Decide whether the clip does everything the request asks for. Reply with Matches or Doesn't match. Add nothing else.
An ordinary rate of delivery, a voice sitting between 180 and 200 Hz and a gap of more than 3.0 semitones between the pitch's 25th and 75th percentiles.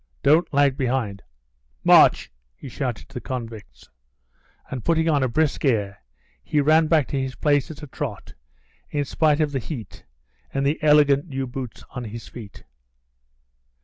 Doesn't match